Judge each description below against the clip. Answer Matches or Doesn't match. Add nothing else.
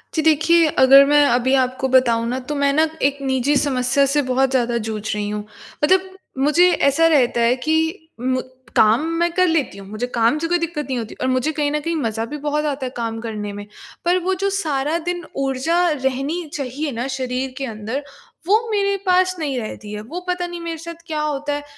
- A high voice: Matches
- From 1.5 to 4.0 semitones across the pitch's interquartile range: Doesn't match